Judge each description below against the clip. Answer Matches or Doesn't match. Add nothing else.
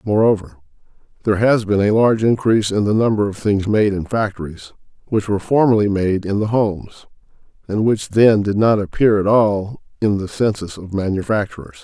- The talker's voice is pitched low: Matches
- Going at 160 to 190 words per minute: Matches